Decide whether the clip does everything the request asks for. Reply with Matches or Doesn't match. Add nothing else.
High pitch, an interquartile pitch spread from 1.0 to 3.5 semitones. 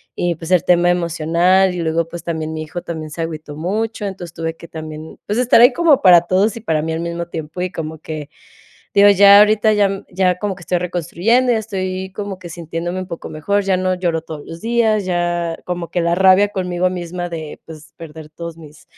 Doesn't match